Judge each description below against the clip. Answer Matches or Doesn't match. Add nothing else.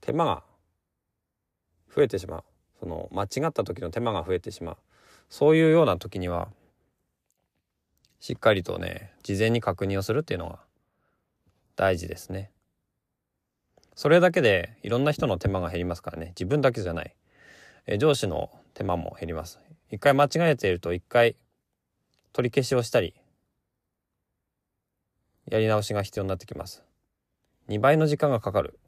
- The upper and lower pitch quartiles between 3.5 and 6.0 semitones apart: Matches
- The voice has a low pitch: Matches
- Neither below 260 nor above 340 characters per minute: Matches